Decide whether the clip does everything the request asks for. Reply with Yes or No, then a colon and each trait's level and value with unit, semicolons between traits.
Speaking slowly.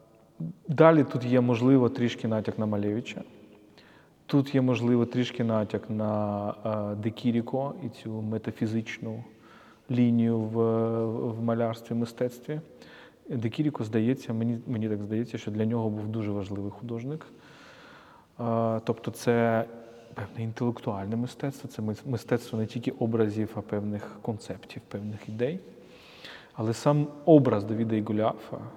No: average, 120 wpm